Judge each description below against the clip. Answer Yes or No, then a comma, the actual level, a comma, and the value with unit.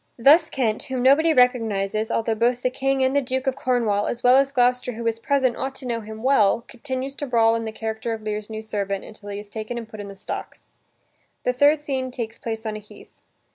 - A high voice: Yes, high, 235 Hz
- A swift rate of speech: Yes, fast, 235 wpm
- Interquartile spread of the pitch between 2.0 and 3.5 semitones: Yes, average, 3.2 semitones